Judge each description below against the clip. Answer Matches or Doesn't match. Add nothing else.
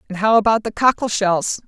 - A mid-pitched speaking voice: Doesn't match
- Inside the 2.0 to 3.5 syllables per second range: Doesn't match